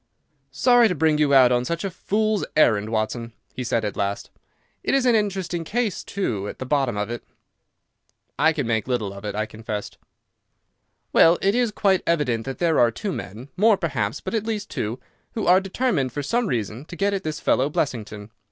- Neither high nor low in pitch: Yes, medium, 145 Hz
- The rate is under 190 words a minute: No, average, 195 wpm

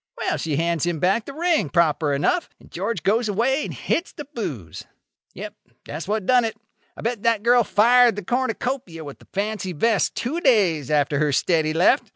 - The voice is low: No, high, 205 Hz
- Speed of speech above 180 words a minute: Yes, average, 195 wpm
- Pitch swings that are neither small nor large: No, wide, 7.1 semitones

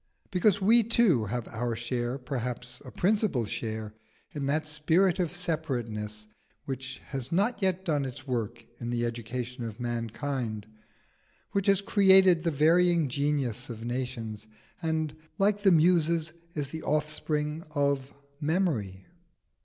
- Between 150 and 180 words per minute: No, slow, 135 wpm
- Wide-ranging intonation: Yes, wide, 6.1 semitones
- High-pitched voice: No, medium, 145 Hz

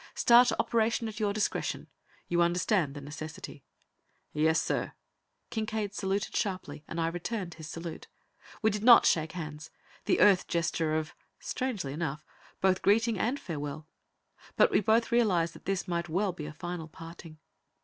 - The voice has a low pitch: No, medium, 175 Hz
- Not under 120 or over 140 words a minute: No, average, 155 wpm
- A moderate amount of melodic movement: Yes, average, 5.0 semitones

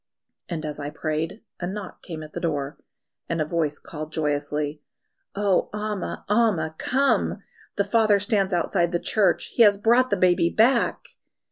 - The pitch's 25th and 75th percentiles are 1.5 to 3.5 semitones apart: No, average, 5.0 semitones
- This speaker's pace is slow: No, average, 160 wpm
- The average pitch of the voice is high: No, medium, 175 Hz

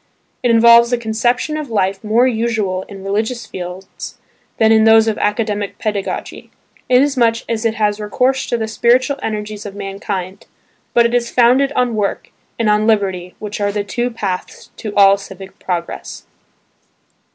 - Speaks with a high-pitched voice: Yes, high, 220 Hz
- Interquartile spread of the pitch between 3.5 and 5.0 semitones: No, average, 2.8 semitones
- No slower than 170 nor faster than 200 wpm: No, average, 160 wpm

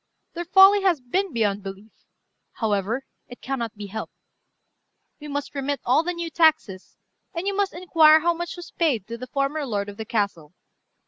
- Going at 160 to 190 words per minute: Yes, average, 180 wpm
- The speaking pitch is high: Yes, very high, 275 Hz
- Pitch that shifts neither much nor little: No, wide, 7.8 semitones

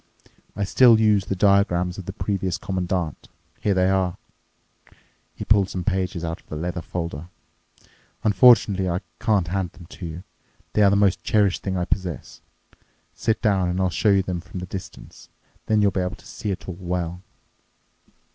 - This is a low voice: Yes, very low, 95 Hz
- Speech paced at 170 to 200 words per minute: Yes, average, 180 wpm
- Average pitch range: No, narrow, 2.2 semitones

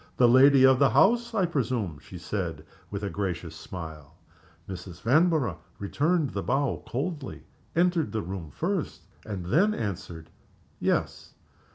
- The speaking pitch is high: No, low, 115 Hz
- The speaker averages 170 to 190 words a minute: No, average, 140 wpm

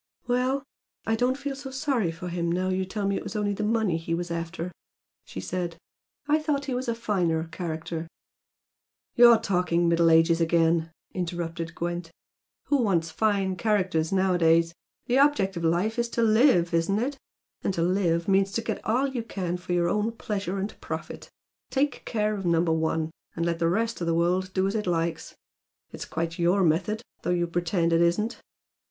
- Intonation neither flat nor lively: Yes, average, 4.6 semitones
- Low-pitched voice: No, medium, 180 Hz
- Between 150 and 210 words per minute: Yes, average, 190 wpm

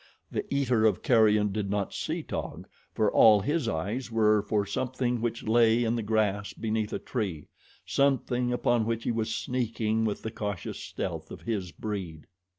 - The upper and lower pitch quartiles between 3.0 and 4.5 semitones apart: No, narrow, 2.5 semitones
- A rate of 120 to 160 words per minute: No, average, 170 wpm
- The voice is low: Yes, low, 110 Hz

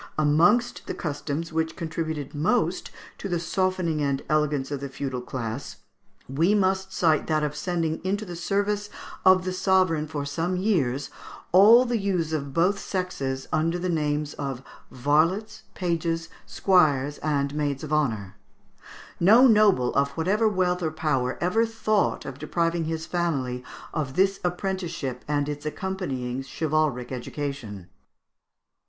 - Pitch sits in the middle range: Yes, medium, 160 Hz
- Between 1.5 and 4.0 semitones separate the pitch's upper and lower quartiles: No, average, 4.7 semitones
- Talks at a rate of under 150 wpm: Yes, average, 140 wpm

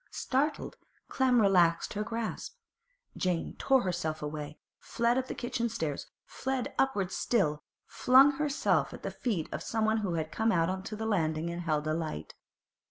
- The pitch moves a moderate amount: No, wide, 6.5 semitones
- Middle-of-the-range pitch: No, high, 200 Hz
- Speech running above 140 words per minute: Yes, average, 165 wpm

